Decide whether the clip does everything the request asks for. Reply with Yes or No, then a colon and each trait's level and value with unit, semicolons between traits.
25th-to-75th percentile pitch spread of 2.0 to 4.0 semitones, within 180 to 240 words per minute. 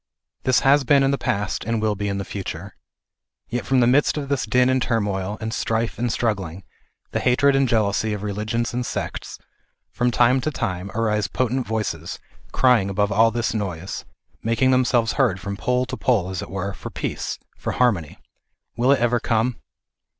Yes: average, 3.7 semitones; average, 190 wpm